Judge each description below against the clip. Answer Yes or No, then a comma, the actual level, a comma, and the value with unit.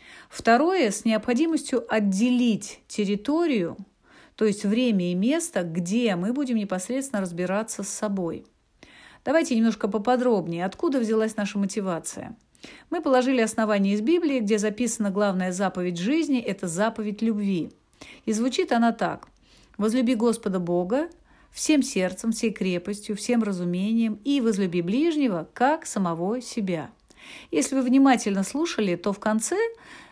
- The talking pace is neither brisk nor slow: Yes, average, 125 wpm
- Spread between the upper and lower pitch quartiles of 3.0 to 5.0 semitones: Yes, average, 4.4 semitones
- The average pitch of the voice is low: No, high, 220 Hz